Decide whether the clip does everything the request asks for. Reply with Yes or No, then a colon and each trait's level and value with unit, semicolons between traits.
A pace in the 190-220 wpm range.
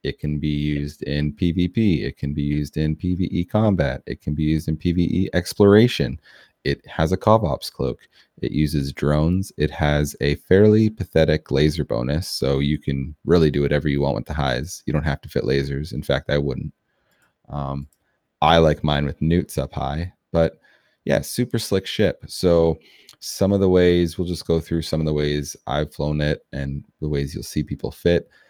Yes: average, 195 wpm